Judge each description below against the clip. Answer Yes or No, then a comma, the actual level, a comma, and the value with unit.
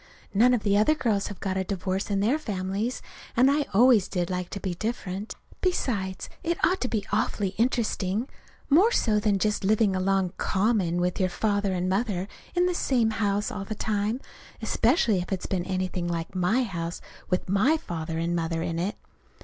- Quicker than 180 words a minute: Yes, average, 190 wpm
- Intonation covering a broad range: No, average, 3.6 semitones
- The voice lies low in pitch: No, high, 200 Hz